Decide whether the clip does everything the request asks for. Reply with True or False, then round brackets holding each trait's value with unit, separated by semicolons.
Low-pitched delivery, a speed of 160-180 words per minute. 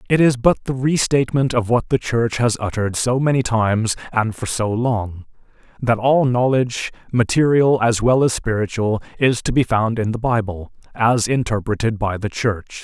True (115 Hz; 175 wpm)